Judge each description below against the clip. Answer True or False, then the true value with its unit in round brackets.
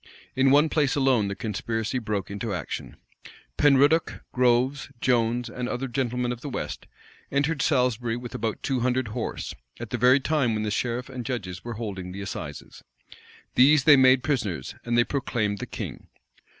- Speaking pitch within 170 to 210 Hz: False (125 Hz)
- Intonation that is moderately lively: True (3.0 semitones)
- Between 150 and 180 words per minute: True (170 wpm)